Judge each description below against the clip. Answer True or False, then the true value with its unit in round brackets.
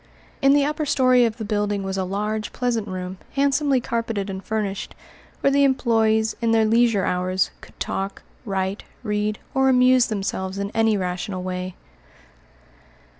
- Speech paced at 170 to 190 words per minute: False (155 wpm)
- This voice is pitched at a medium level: False (215 Hz)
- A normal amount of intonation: True (4.2 semitones)